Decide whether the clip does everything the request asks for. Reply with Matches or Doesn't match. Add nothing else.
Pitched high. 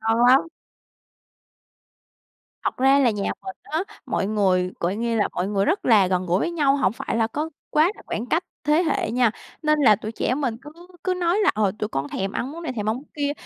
Matches